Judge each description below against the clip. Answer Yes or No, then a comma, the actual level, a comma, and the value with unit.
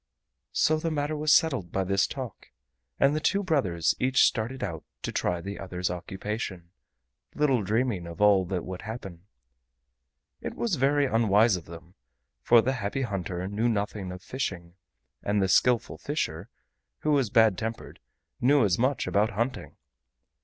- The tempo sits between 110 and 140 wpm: No, average, 160 wpm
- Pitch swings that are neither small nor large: No, wide, 6.1 semitones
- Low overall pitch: Yes, low, 105 Hz